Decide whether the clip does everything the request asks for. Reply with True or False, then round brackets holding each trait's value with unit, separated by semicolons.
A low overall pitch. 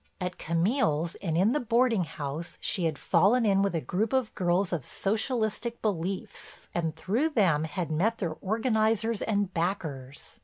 False (195 Hz)